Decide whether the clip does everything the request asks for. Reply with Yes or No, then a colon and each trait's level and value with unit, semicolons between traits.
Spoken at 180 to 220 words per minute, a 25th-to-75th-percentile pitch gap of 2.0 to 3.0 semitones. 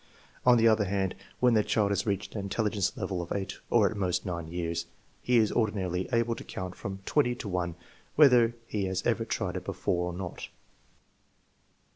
No: average, 190 wpm; average, 3.8 semitones